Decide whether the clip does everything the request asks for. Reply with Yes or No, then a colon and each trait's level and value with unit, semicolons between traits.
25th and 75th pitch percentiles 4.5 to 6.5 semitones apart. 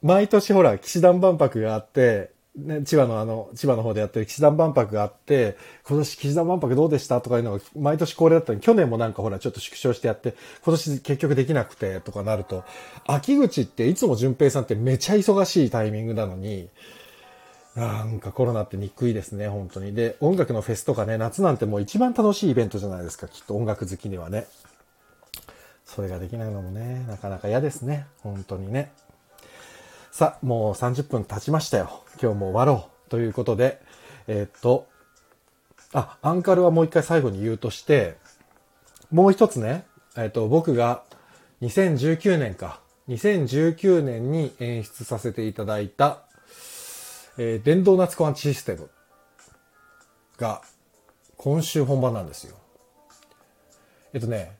Yes: wide, 6.1 semitones